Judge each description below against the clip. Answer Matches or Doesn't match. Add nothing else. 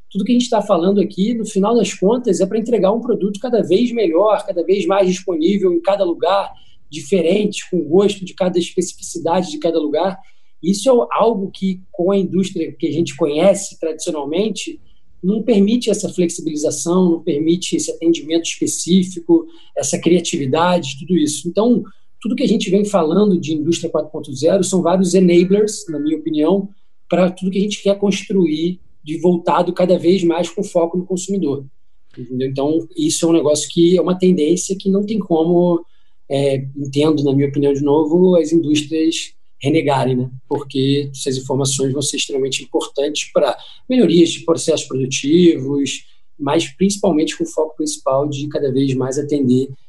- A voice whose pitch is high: Doesn't match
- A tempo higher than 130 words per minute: Matches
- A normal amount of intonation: Matches